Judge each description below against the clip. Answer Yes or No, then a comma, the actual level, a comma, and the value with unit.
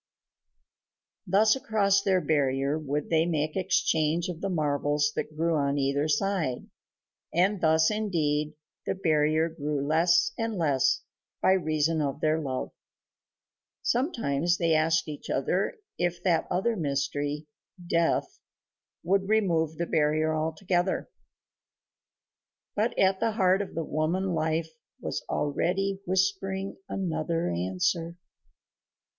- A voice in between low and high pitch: Yes, medium, 165 Hz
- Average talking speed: No, slow, 120 wpm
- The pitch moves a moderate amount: Yes, average, 3.9 semitones